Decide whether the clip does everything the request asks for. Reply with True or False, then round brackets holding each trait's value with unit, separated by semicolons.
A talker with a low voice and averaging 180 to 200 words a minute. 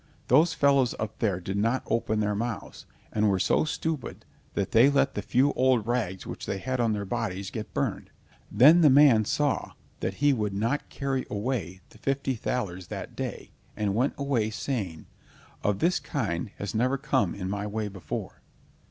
True (115 Hz; 185 wpm)